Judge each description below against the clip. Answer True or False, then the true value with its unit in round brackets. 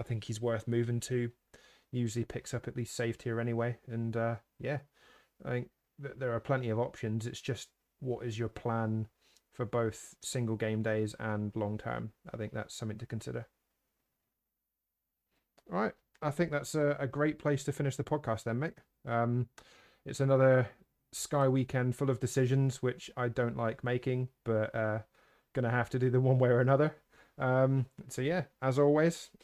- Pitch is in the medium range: False (120 Hz)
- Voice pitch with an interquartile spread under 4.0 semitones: True (2.7 semitones)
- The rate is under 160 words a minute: False (180 wpm)